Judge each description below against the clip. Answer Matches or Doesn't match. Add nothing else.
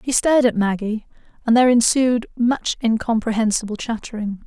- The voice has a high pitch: Matches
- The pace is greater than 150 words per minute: Doesn't match